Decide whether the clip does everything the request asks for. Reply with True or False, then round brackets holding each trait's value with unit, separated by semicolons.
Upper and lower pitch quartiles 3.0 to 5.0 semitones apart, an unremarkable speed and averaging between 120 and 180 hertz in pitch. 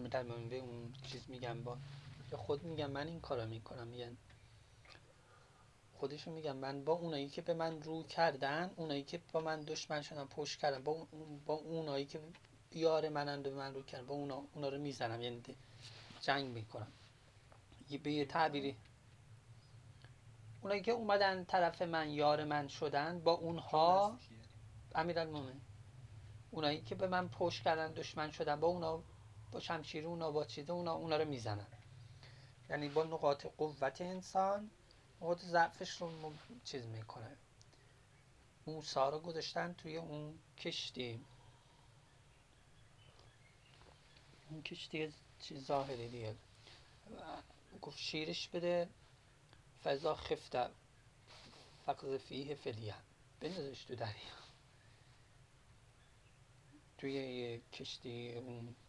True (4.4 semitones; 120 wpm; 135 Hz)